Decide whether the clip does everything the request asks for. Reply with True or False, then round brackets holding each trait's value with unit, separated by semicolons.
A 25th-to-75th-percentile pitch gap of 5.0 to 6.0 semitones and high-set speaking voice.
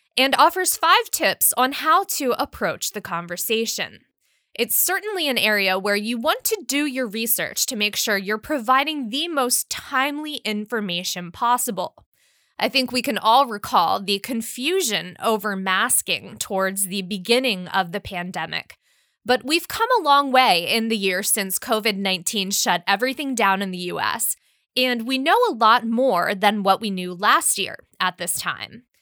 True (5.6 semitones; 230 Hz)